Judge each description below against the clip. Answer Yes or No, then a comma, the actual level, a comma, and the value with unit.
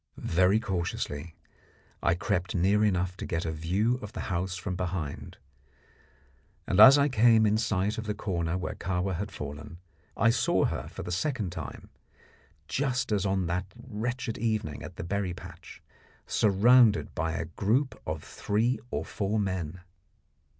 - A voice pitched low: Yes, very low, 95 Hz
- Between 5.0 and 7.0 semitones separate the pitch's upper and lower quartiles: No, average, 4.1 semitones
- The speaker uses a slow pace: No, average, 155 wpm